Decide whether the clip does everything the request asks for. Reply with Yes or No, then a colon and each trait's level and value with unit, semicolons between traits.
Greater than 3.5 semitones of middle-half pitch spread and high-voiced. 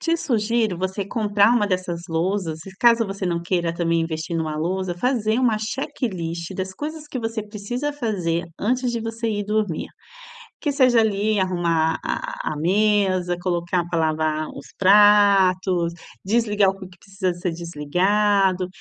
Yes: average, 4.0 semitones; high, 195 Hz